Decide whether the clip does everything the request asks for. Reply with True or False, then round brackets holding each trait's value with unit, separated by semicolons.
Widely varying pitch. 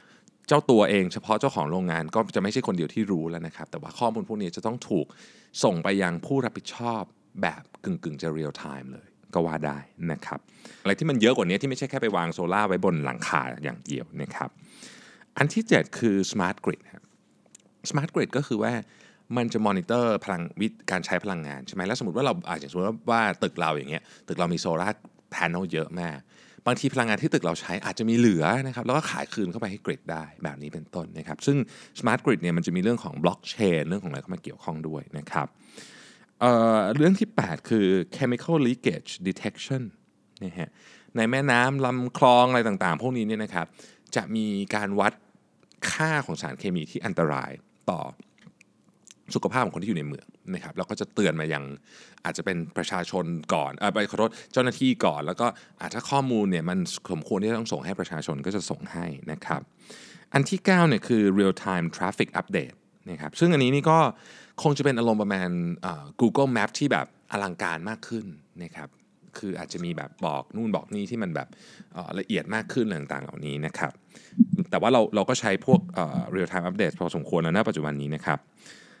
True (7.0 semitones)